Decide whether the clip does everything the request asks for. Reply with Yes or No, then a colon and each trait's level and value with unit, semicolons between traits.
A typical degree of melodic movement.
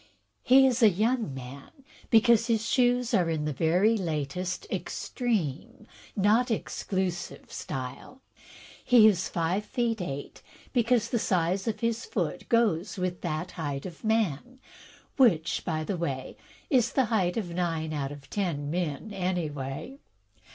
No: wide, 6.4 semitones